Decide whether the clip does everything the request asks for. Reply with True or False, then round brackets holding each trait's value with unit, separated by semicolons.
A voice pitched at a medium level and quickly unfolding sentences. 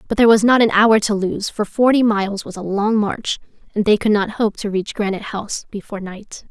False (210 Hz; 240 wpm)